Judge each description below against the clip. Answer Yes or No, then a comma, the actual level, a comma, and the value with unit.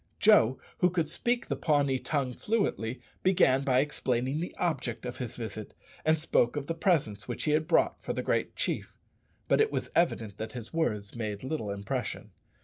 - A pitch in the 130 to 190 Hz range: Yes, low, 135 Hz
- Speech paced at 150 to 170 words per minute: No, average, 185 wpm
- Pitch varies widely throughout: Yes, wide, 5.8 semitones